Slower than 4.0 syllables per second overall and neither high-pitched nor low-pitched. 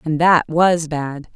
Yes: 3.4 syllables/s; medium, 160 Hz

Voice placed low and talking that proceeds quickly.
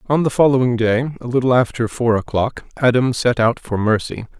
No: low, 120 Hz; average, 190 wpm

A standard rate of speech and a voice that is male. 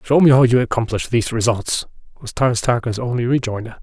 Yes: average, 190 wpm; male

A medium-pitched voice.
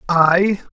Yes: medium, 180 Hz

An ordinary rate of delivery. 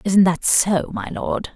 Yes: average, 195 wpm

